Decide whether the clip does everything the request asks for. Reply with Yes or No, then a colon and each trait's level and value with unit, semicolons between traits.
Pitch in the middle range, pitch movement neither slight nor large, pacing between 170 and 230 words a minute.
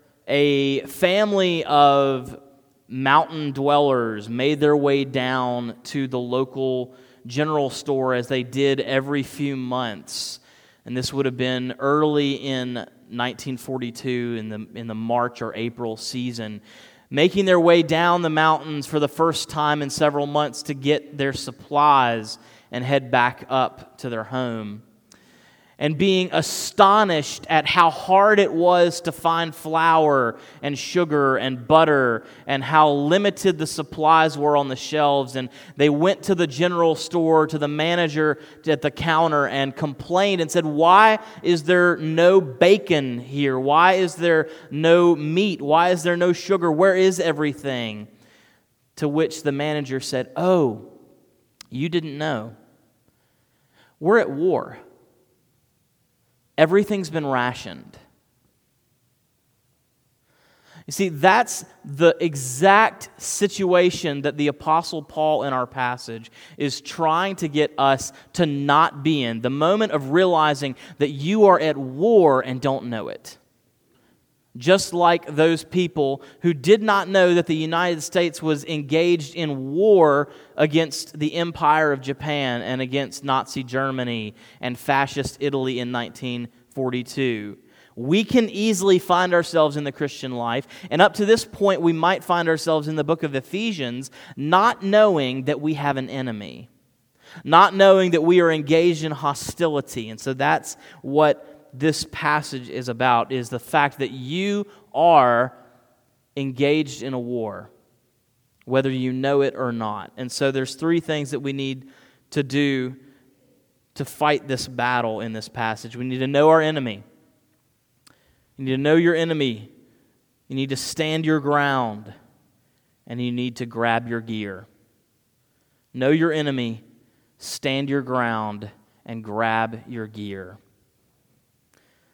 No: medium, 145 Hz; average, 4.3 semitones; average, 145 wpm